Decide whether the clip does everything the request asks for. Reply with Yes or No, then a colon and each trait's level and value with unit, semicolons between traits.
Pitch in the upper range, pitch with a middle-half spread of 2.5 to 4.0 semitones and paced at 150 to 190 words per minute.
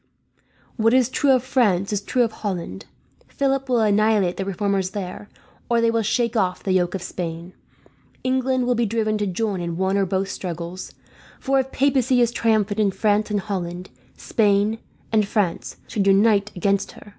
Yes: high, 210 Hz; average, 3.5 semitones; average, 180 wpm